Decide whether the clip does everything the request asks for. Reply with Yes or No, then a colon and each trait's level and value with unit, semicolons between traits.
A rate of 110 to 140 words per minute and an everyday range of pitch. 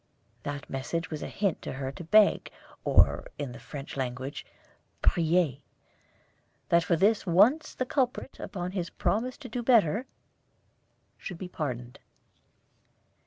No: slow, 135 wpm; wide, 7.0 semitones